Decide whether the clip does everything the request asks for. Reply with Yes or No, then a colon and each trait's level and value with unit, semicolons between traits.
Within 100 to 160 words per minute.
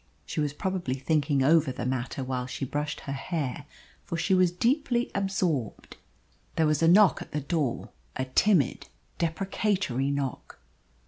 Yes: average, 150 wpm